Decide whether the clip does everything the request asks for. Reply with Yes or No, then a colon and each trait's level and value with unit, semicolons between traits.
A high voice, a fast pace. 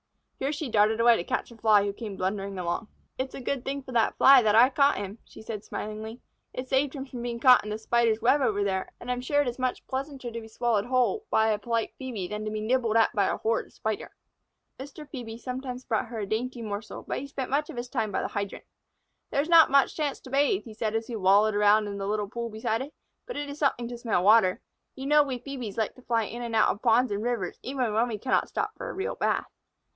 Yes: high, 235 Hz; fast, 260 wpm